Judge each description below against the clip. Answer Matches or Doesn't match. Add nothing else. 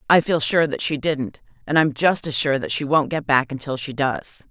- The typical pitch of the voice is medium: Matches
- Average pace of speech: Doesn't match